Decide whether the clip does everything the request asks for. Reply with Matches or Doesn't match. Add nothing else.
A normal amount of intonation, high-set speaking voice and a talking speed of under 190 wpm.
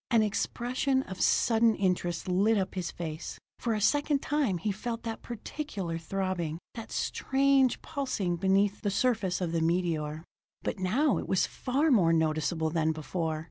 Doesn't match